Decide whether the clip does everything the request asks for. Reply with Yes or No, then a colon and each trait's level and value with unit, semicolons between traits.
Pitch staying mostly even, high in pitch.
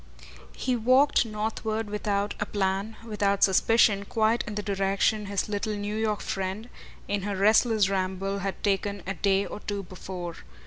Yes: narrow, 1.8 semitones; high, 205 Hz